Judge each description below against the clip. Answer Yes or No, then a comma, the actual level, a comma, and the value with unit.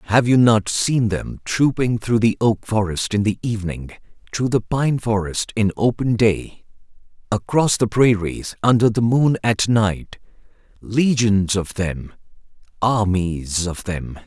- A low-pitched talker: Yes, low, 110 Hz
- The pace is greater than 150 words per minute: No, average, 145 wpm